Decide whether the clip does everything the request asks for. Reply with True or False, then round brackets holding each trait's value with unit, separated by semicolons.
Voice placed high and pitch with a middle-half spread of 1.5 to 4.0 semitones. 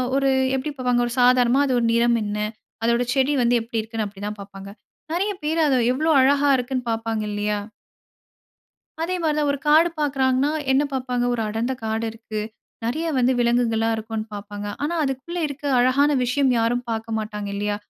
True (245 Hz; 3.7 semitones)